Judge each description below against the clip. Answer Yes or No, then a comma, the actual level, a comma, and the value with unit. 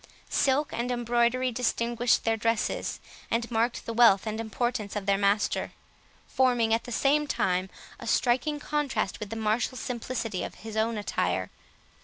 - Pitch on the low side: No, high, 230 Hz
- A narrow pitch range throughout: Yes, narrow, 2.3 semitones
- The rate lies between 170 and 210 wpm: No, average, 155 wpm